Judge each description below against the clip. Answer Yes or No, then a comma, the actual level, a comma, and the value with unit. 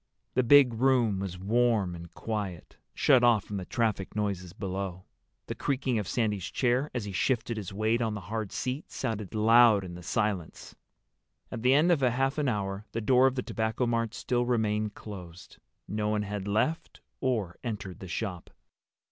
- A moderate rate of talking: Yes, average, 180 wpm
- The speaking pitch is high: No, low, 110 Hz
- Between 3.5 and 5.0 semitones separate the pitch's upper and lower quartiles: Yes, average, 3.8 semitones